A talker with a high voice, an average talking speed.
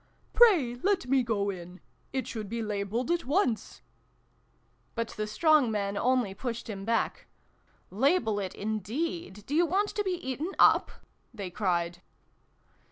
Yes: high, 230 Hz; average, 160 wpm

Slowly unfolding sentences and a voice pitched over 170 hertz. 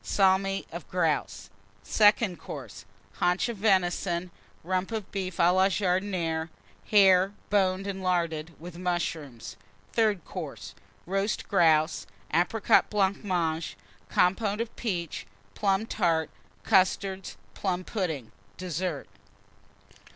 Yes: slow, 105 wpm; medium, 185 Hz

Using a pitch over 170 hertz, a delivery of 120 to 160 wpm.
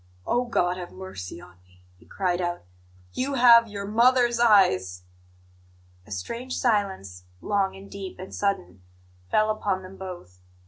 Yes: high, 190 Hz; average, 145 wpm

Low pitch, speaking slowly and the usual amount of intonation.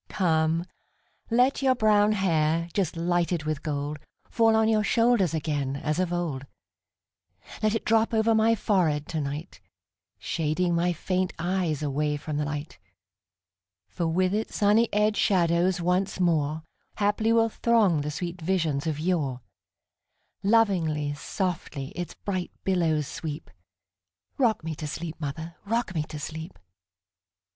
No: medium, 170 Hz; slow, 120 wpm; average, 5.0 semitones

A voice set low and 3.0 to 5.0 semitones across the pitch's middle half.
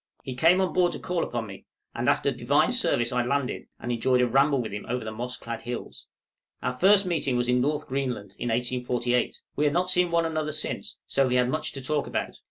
Yes: low, 130 Hz; average, 4.0 semitones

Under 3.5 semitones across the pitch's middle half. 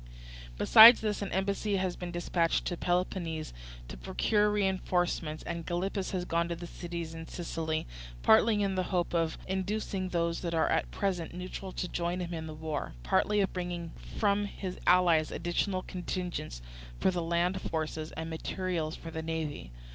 Yes: narrow, 2.5 semitones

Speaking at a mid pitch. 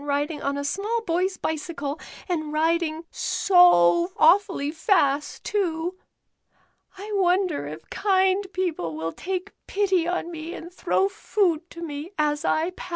No: very high, 335 Hz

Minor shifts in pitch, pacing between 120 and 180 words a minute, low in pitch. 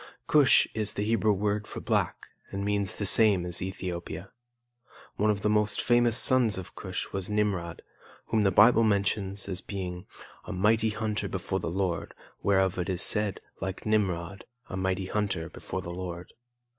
Yes: narrow, 2.3 semitones; average, 170 wpm; low, 100 Hz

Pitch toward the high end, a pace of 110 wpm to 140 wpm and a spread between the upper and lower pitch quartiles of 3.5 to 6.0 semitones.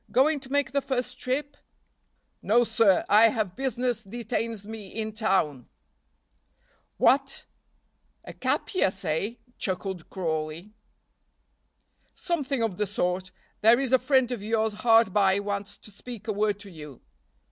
Yes: high, 220 Hz; slow, 135 wpm; average, 4.2 semitones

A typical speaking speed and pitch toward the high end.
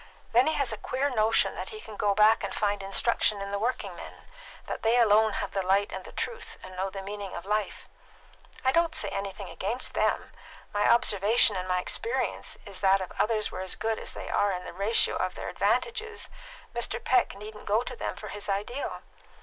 No: fast, 215 wpm; high, 210 Hz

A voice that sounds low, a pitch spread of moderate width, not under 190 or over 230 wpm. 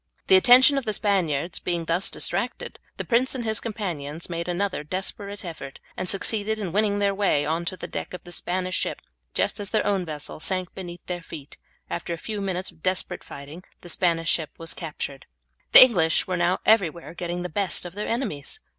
No: medium, 180 Hz; average, 3.3 semitones; average, 200 wpm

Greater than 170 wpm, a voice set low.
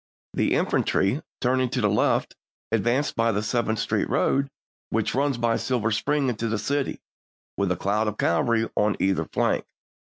No: average, 165 wpm; low, 115 Hz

